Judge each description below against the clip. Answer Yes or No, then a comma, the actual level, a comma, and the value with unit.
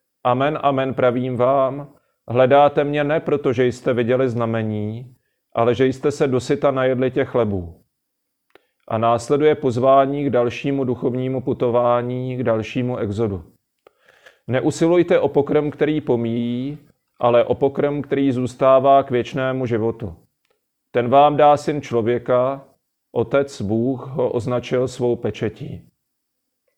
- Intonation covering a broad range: No, average, 2.7 semitones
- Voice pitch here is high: No, low, 130 Hz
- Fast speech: No, average, 120 wpm